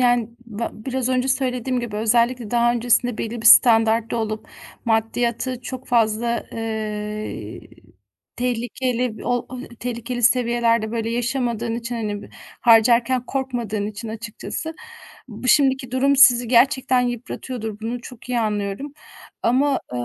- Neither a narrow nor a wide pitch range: No, narrow, 2.0 semitones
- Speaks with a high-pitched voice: Yes, high, 235 Hz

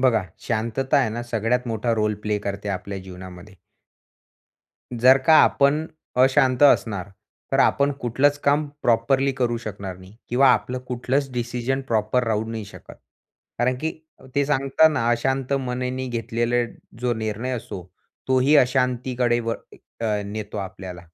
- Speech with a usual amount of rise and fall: Yes, average, 3.4 semitones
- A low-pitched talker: Yes, low, 120 Hz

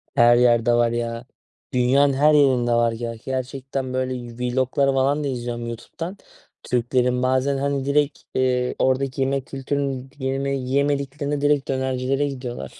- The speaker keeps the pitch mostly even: Yes, narrow, 2.0 semitones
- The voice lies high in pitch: No, low, 130 Hz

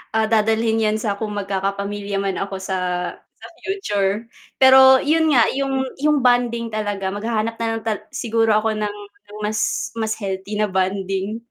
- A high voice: Yes, high, 215 Hz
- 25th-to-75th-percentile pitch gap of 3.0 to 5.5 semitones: No, narrow, 2.6 semitones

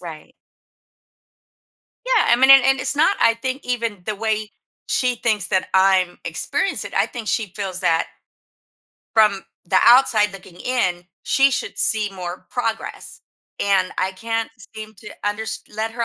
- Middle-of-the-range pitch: No, high, 215 Hz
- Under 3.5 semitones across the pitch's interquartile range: No, average, 4.2 semitones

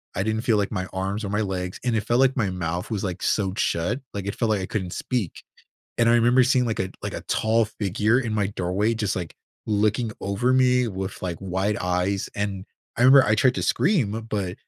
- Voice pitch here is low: Yes, low, 105 Hz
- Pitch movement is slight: No, average, 3.4 semitones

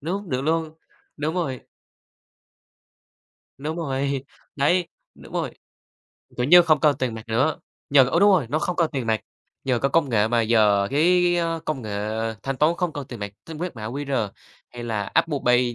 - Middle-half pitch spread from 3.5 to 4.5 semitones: No, average, 5.1 semitones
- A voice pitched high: No, medium, 140 Hz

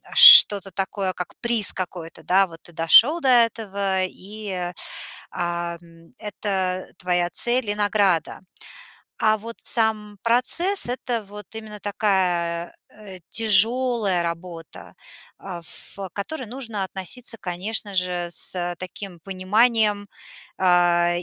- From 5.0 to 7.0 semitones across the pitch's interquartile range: No, average, 3.8 semitones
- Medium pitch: No, high, 195 Hz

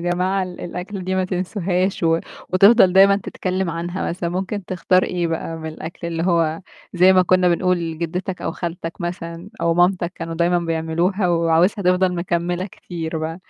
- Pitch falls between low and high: Yes, medium, 175 Hz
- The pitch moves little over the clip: Yes, narrow, 1.7 semitones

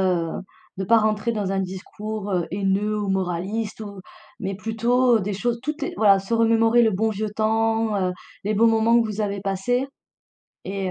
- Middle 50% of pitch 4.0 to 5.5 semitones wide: No, narrow, 2.6 semitones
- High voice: Yes, high, 215 Hz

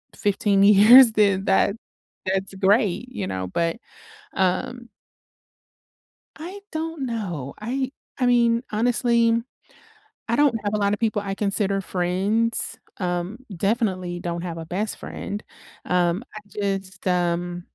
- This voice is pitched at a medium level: No, high, 200 Hz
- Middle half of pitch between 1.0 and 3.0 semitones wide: No, average, 4.1 semitones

